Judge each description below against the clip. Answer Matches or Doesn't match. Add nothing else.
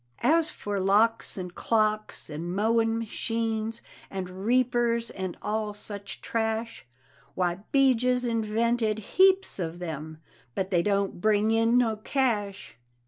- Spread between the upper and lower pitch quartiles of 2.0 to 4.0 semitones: Matches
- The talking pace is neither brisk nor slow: Doesn't match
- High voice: Matches